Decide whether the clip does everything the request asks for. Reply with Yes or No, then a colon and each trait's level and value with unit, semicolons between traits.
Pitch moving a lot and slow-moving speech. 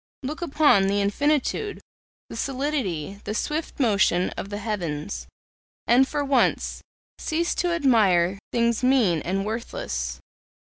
Yes: wide, 6.6 semitones; slow, 125 wpm